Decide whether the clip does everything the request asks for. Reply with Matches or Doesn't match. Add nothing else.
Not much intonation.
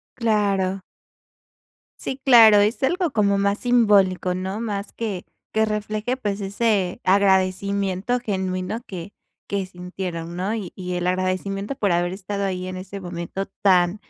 Matches